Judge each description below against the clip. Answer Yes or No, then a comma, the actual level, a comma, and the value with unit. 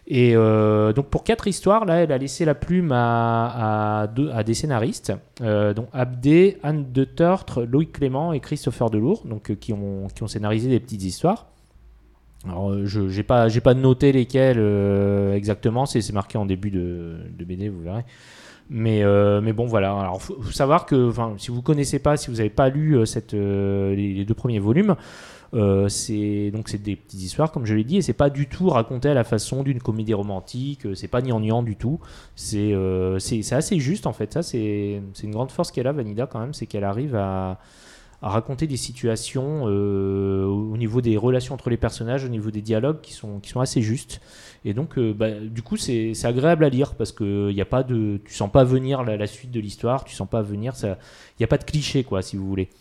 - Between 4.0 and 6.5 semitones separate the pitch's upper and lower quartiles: Yes, average, 4.6 semitones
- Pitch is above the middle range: No, low, 115 Hz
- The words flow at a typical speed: No, fast, 230 wpm